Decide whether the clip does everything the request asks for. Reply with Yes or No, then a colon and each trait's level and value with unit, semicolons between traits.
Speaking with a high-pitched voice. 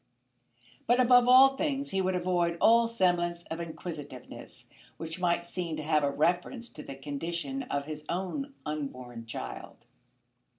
No: medium, 175 Hz